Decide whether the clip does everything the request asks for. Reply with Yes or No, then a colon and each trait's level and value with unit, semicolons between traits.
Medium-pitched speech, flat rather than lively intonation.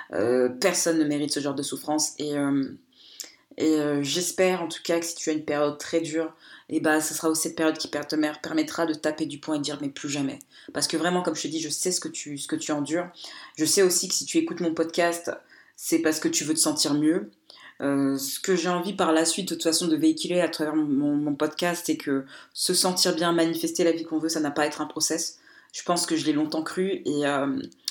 Yes: medium, 155 Hz; narrow, 2.2 semitones